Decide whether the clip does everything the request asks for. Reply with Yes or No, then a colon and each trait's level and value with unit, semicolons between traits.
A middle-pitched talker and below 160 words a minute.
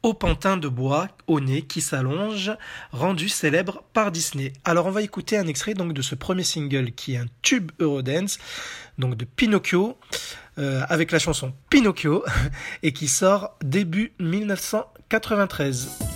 Yes: medium, 170 Hz; average, 150 wpm